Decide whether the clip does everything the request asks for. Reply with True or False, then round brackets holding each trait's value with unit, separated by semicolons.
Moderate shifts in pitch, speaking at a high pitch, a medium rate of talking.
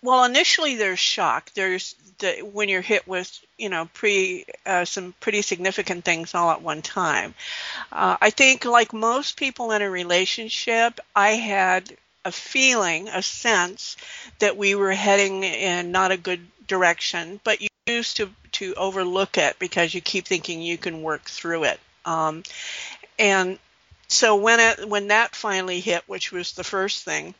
True (3.3 semitones; 195 Hz; 165 wpm)